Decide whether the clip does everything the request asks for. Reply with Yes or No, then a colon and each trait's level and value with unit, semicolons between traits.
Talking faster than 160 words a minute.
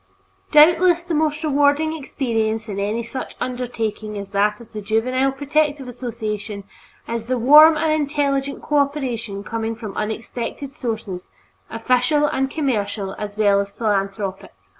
No: slow, 135 wpm